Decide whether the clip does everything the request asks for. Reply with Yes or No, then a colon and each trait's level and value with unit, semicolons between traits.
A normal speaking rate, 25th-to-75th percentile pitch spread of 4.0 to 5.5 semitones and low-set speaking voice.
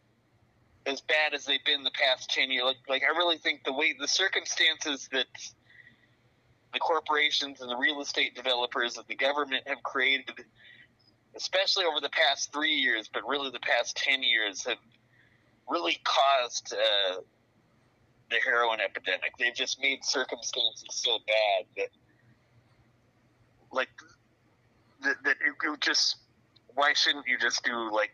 No: average, 145 wpm; average, 3.2 semitones; low, 125 Hz